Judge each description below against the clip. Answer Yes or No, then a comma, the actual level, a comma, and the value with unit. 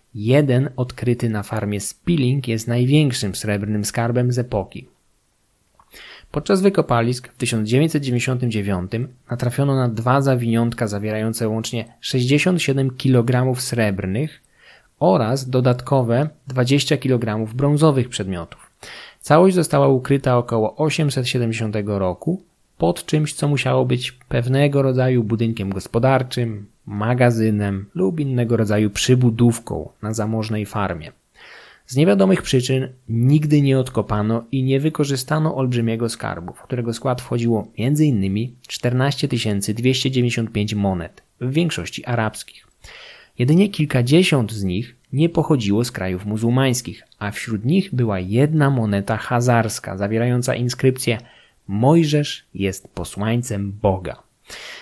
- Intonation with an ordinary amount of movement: Yes, average, 3.7 semitones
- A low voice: Yes, low, 125 Hz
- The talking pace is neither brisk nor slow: No, slow, 105 wpm